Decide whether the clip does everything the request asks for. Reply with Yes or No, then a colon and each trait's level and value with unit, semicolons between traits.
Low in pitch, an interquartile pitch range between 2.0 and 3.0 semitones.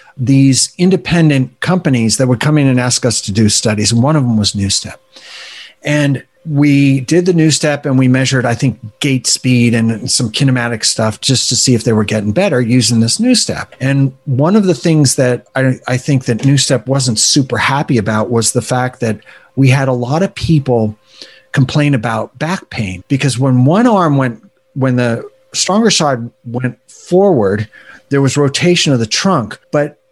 No: low, 130 Hz; average, 3.8 semitones